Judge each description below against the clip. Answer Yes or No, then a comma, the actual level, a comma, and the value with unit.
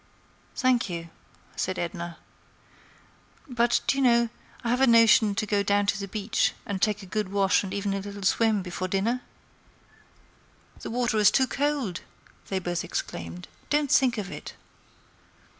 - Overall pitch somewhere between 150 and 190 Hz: No, high, 205 Hz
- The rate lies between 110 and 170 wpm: Yes, average, 160 wpm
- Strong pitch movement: No, average, 3.8 semitones